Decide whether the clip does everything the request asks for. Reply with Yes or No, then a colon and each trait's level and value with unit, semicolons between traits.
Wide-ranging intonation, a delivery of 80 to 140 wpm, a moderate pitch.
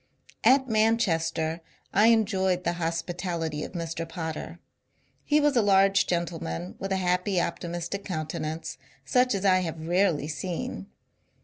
No: average, 3.3 semitones; slow, 135 wpm; medium, 175 Hz